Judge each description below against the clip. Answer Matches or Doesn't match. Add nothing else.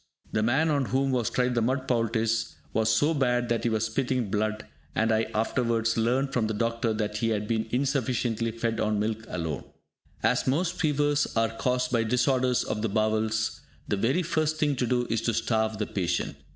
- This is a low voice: Matches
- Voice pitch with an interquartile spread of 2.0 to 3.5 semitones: Matches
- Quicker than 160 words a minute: Matches